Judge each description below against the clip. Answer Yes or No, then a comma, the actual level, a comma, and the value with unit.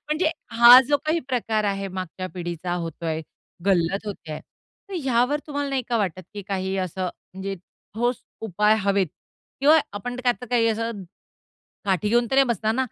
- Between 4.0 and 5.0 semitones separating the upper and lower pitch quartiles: Yes, average, 4.7 semitones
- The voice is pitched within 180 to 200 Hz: No, high, 210 Hz